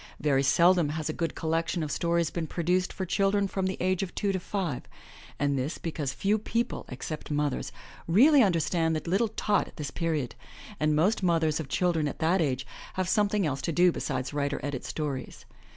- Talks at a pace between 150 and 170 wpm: No, average, 200 wpm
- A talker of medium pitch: Yes, medium, 165 Hz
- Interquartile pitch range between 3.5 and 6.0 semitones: Yes, average, 4.0 semitones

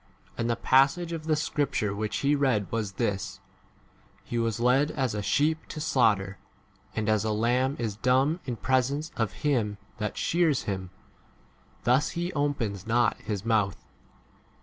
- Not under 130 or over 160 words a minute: Yes, average, 155 wpm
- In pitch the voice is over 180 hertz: No, low, 120 Hz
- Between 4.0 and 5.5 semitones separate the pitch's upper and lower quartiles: Yes, average, 5.1 semitones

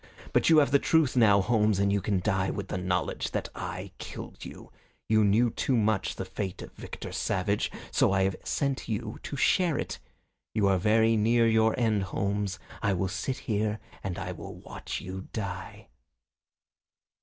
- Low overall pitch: Yes, low, 105 Hz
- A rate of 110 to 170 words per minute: No, average, 185 wpm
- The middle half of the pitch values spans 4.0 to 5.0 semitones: No, average, 2.9 semitones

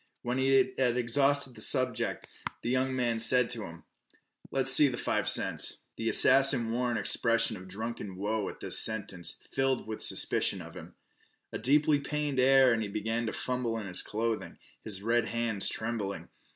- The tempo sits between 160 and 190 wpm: Yes, average, 180 wpm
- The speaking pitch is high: No, low, 120 Hz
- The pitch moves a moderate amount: Yes, average, 3.0 semitones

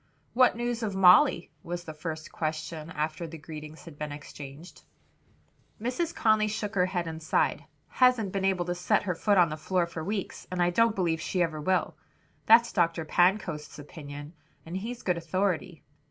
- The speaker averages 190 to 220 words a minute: No, average, 180 wpm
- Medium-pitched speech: Yes, medium, 175 Hz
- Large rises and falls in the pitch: No, average, 4.0 semitones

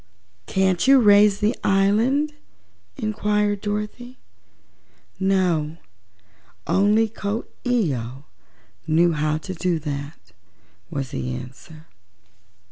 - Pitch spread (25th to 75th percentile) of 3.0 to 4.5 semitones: No, wide, 5.5 semitones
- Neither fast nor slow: No, slow, 95 wpm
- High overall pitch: Yes, high, 195 Hz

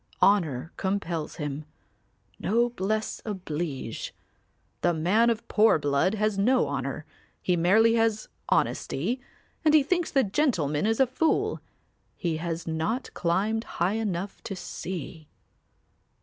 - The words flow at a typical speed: No, slow, 120 wpm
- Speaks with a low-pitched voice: No, high, 195 Hz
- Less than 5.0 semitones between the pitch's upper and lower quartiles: No, average, 5.3 semitones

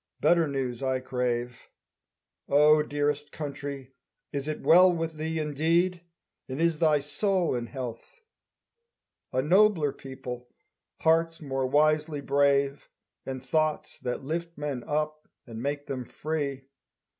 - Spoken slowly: Yes, slow, 125 wpm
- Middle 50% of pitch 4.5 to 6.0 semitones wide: No, average, 3.1 semitones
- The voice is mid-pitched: Yes, medium, 145 Hz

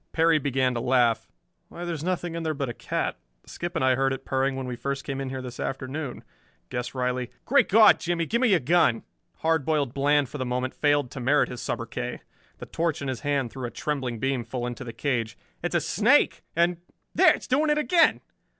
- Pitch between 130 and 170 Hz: Yes, low, 135 Hz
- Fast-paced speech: Yes, fast, 225 wpm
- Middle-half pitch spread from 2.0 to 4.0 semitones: No, average, 4.4 semitones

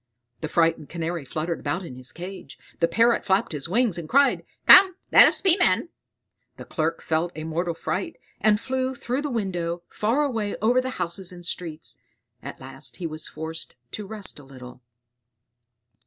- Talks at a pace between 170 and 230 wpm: Yes, average, 175 wpm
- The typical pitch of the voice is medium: Yes, medium, 175 Hz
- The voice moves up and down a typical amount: No, wide, 5.7 semitones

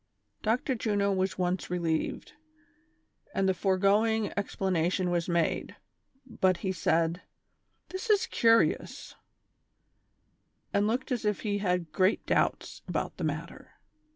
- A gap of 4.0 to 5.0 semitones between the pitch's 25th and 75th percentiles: No, average, 3.5 semitones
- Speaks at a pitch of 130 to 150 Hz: No, high, 195 Hz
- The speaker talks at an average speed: No, slow, 130 wpm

